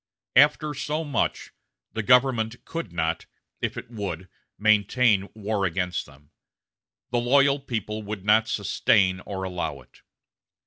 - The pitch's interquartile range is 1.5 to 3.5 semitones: No, average, 4.8 semitones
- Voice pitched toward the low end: Yes, low, 110 Hz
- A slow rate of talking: Yes, slow, 130 wpm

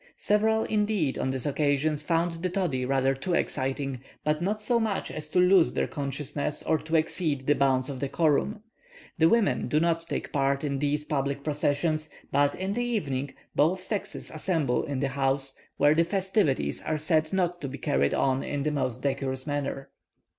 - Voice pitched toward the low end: No, medium, 150 Hz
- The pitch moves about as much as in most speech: Yes, average, 4.1 semitones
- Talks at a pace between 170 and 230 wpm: Yes, average, 180 wpm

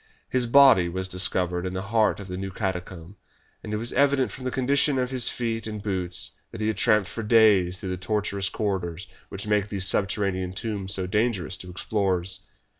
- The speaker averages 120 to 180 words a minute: No, average, 195 wpm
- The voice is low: Yes, low, 100 Hz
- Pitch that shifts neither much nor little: Yes, average, 3.2 semitones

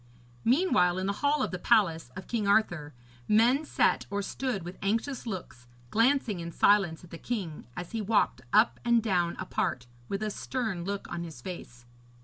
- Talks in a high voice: Yes, high, 200 Hz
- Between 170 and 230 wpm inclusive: Yes, average, 180 wpm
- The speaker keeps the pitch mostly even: No, average, 4.9 semitones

